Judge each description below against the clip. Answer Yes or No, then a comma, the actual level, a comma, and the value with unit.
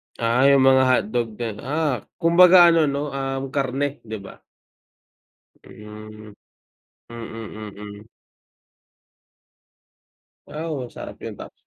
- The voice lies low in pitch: Yes, low, 130 Hz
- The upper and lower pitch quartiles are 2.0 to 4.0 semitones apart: No, average, 4.7 semitones